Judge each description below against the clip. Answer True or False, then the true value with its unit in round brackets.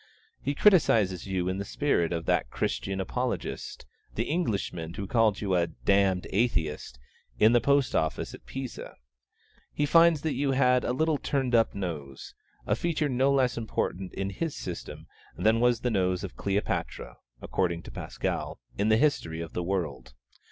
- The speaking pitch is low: True (105 Hz)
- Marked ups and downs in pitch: True (6.4 semitones)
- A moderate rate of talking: True (165 wpm)